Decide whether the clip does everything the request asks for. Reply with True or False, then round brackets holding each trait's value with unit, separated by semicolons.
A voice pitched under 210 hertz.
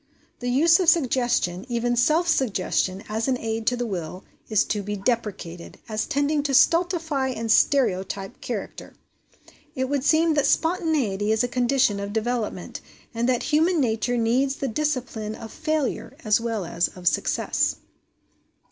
False (245 Hz)